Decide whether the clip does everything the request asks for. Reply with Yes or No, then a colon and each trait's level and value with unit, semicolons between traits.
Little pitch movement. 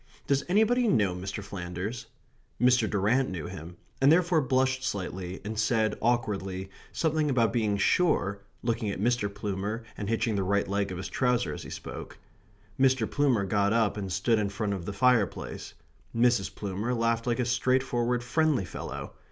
No: average, 4.0 semitones